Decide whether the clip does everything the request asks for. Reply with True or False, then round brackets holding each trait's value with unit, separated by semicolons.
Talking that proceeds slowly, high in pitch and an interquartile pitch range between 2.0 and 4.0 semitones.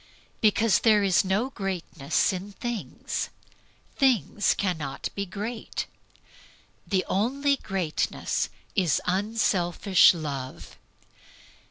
True (85 wpm; 195 Hz; 3.7 semitones)